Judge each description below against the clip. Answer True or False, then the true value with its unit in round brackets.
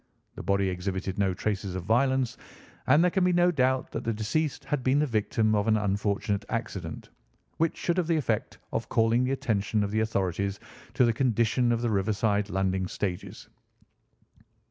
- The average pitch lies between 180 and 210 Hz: False (110 Hz)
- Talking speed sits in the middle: True (180 wpm)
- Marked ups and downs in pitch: False (4.6 semitones)